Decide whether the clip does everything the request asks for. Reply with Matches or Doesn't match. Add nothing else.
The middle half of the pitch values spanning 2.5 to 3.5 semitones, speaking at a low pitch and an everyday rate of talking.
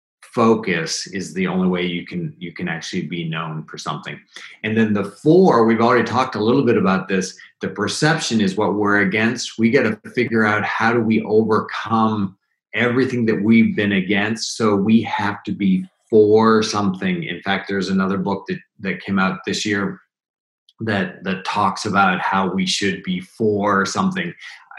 Matches